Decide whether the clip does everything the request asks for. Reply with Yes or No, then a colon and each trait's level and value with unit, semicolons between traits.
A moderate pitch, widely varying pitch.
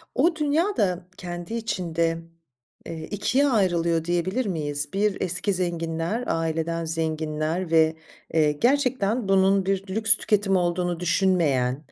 No: medium, 175 Hz; average, 3.9 semitones